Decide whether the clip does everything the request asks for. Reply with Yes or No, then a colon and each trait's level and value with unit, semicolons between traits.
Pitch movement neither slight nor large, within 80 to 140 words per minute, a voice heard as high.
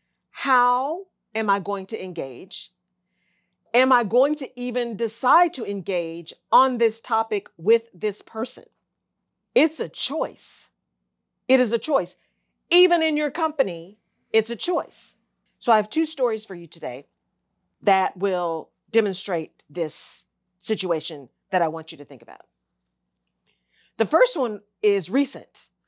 No: wide, 7.0 semitones; slow, 135 wpm; high, 215 Hz